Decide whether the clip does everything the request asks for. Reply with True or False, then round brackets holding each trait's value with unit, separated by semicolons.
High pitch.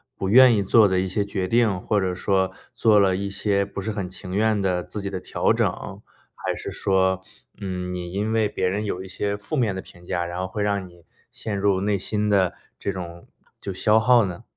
False (100 Hz)